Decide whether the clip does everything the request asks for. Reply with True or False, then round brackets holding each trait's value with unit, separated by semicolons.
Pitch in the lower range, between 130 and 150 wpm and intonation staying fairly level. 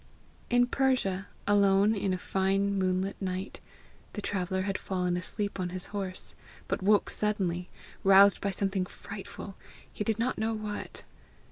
False (195 Hz; 145 wpm; 1.7 semitones)